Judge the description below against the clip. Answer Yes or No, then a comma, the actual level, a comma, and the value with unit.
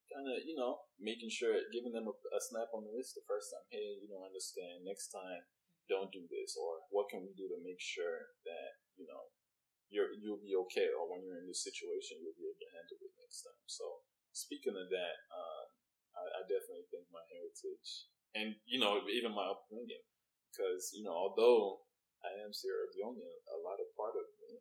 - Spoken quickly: Yes, fast, 210 wpm